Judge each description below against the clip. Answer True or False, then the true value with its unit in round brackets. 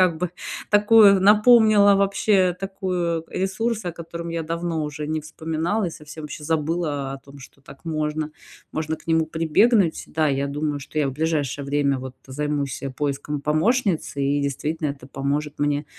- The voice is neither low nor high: True (155 Hz)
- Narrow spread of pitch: False (3.7 semitones)